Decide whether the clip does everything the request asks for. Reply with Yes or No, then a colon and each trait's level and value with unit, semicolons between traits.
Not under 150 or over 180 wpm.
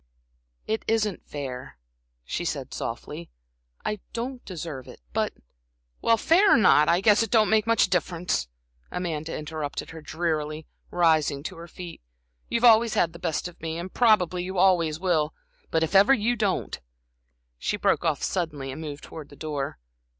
Yes: average, 165 wpm